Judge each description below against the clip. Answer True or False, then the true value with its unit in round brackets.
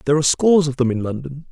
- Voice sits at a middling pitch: True (145 Hz)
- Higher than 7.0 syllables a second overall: True (8.1 syllables/s)